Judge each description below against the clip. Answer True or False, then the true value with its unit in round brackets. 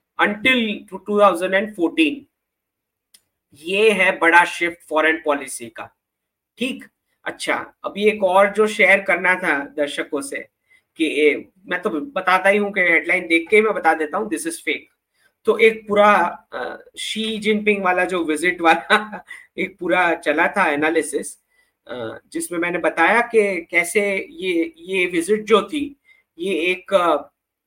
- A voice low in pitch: False (195 Hz)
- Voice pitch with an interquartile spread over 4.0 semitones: True (4.9 semitones)